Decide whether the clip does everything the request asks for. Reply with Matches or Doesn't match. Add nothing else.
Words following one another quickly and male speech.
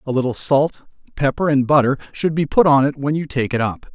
Matches